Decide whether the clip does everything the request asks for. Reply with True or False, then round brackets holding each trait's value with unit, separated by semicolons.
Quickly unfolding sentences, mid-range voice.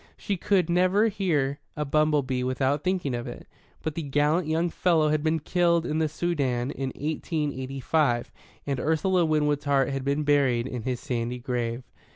False (185 wpm; 150 Hz)